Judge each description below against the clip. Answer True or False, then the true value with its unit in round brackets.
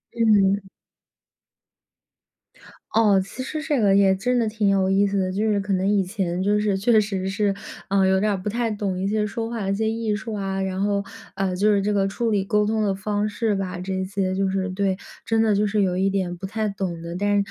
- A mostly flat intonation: True (1.8 semitones)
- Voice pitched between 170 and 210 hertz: True (200 Hz)